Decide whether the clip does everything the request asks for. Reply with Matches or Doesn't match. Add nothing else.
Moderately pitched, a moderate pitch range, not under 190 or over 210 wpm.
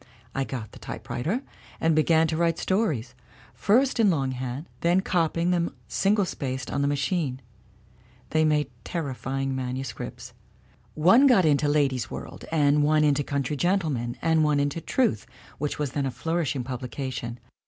Doesn't match